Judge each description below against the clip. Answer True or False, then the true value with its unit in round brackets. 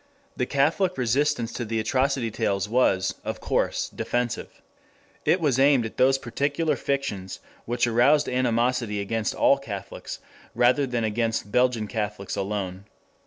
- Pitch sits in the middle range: False (120 Hz)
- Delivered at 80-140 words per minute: True (135 wpm)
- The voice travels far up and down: False (4.1 semitones)